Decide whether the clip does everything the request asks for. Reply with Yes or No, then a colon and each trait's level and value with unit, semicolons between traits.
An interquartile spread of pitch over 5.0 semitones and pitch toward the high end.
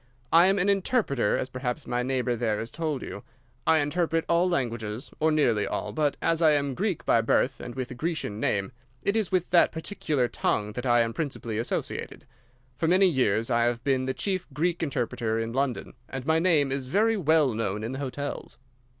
No: wide, 5.6 semitones; low, 135 Hz